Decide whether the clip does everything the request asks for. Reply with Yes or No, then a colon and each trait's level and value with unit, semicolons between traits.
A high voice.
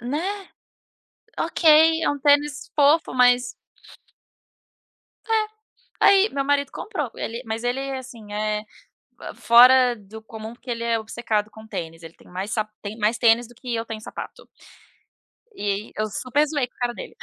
Yes: high, 240 Hz